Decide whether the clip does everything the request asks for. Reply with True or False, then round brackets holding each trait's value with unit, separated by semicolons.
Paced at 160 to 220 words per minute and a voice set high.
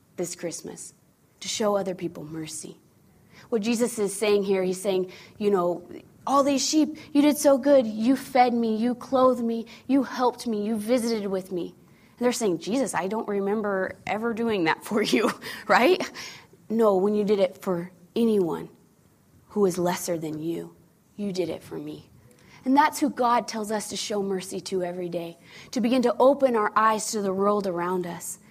True (185 wpm; 205 Hz)